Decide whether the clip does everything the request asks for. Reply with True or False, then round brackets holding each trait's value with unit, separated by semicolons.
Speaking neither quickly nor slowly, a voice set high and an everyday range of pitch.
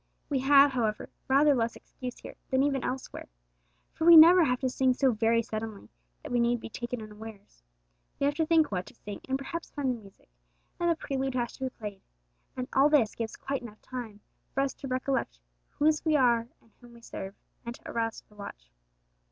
False (210 wpm; 250 Hz; 3.6 semitones)